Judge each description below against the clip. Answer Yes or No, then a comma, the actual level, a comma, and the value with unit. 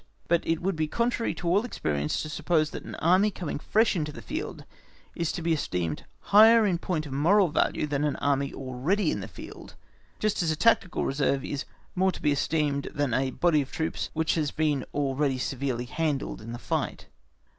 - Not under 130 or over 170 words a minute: No, average, 200 wpm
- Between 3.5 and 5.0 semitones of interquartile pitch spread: Yes, average, 4.3 semitones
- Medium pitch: Yes, medium, 155 Hz